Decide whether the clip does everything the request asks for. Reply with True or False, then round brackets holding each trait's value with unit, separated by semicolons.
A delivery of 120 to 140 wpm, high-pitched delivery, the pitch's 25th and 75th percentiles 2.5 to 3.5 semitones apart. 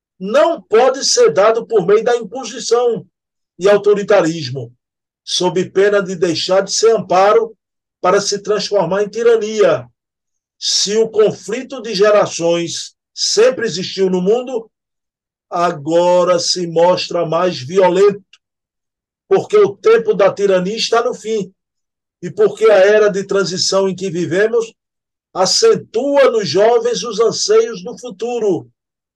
False (125 wpm; 205 Hz; 4.2 semitones)